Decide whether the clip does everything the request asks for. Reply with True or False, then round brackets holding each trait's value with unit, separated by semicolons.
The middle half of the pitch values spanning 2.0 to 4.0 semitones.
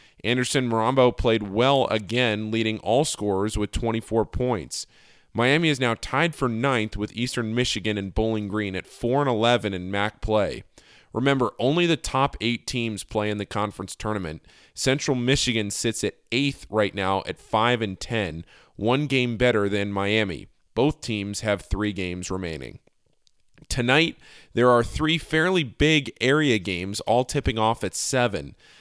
True (3.4 semitones)